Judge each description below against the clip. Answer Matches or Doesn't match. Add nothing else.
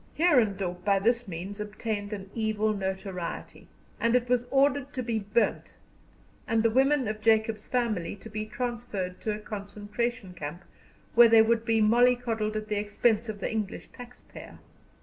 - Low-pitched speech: Doesn't match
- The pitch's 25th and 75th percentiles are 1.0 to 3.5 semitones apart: Matches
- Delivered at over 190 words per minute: Doesn't match